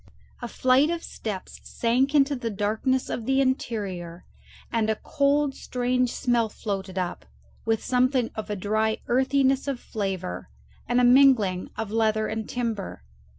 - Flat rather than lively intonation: No, average, 3.8 semitones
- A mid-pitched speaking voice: No, high, 230 Hz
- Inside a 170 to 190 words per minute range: No, average, 150 wpm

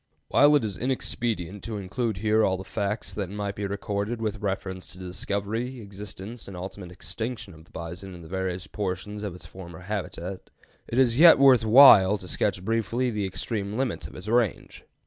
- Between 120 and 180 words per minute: No, average, 190 wpm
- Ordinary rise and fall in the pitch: Yes, average, 3.2 semitones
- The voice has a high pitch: No, low, 100 Hz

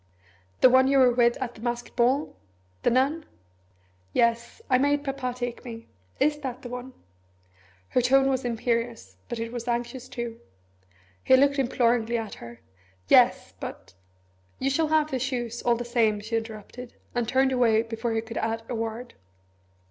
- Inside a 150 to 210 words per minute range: Yes, average, 170 wpm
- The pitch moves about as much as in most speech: No, narrow, 2.2 semitones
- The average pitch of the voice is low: No, high, 240 Hz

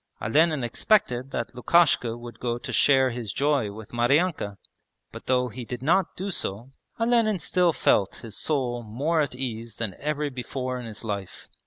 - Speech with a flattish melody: No, average, 4.5 semitones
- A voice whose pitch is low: Yes, low, 125 Hz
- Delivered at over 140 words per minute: Yes, average, 170 wpm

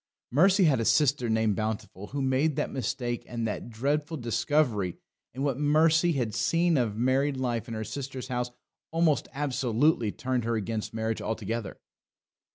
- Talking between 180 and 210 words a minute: No, average, 160 wpm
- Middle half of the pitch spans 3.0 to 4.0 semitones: No, average, 4.5 semitones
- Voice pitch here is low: Yes, low, 125 Hz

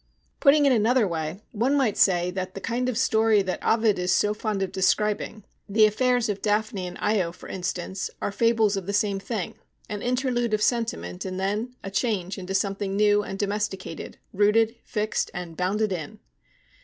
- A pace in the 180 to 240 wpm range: Yes, average, 185 wpm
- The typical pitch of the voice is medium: No, high, 205 Hz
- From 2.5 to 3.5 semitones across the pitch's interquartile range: Yes, average, 2.9 semitones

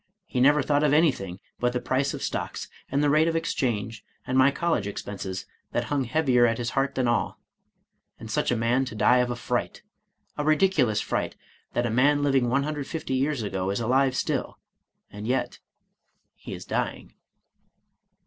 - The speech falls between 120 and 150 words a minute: No, average, 185 wpm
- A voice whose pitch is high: No, low, 130 Hz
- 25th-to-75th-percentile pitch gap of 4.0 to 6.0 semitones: No, average, 3.6 semitones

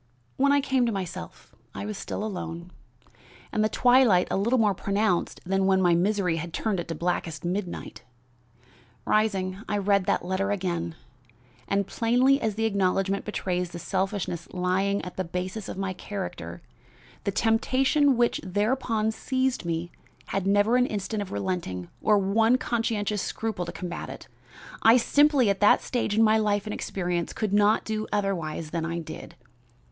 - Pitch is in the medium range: No, high, 200 Hz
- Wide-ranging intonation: No, average, 3.4 semitones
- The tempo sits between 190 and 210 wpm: No, average, 165 wpm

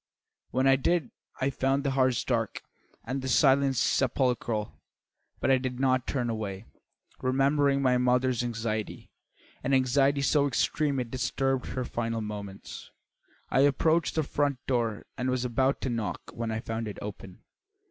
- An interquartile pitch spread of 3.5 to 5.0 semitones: No, average, 2.8 semitones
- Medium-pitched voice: No, low, 130 Hz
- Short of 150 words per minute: No, average, 155 wpm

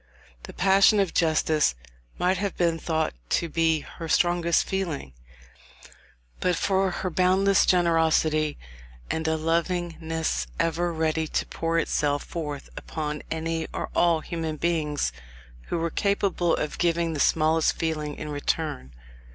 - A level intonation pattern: Yes, narrow, 1.9 semitones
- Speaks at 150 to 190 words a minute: No, slow, 135 wpm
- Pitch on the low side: No, medium, 165 Hz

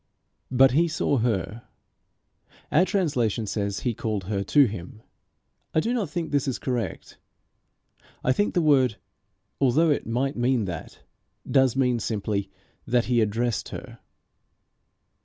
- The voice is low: Yes, low, 125 Hz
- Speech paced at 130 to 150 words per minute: Yes, average, 140 wpm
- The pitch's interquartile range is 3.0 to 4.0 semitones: No, average, 4.8 semitones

